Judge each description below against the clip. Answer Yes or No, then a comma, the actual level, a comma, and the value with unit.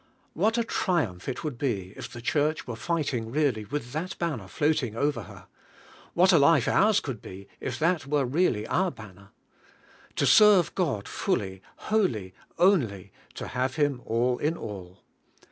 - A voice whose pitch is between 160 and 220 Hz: No, medium, 140 Hz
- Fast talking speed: No, average, 160 wpm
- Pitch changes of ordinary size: No, wide, 7.2 semitones